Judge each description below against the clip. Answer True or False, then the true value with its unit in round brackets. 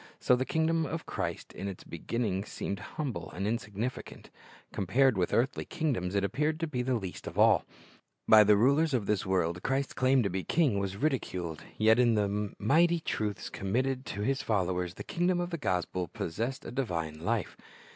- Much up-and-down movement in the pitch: True (6.0 semitones)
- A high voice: False (110 Hz)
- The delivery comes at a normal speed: True (185 wpm)